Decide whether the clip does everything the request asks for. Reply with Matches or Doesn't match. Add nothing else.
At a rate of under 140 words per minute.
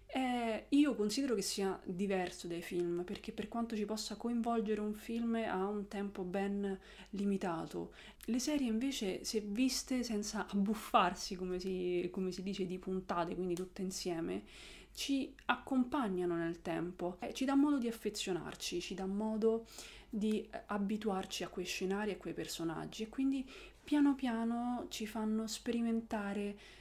Doesn't match